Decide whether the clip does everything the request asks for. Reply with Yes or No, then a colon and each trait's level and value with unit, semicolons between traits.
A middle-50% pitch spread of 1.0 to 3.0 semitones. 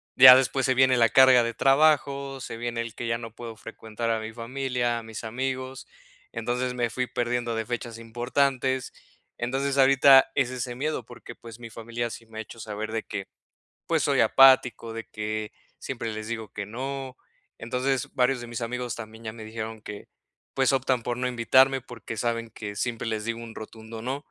Yes: narrow, 2.5 semitones